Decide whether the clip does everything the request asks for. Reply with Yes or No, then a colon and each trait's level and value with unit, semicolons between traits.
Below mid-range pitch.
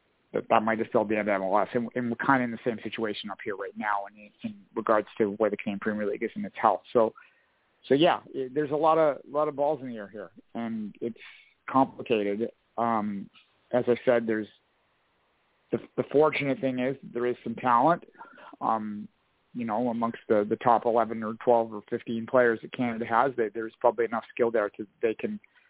Yes: low, 115 Hz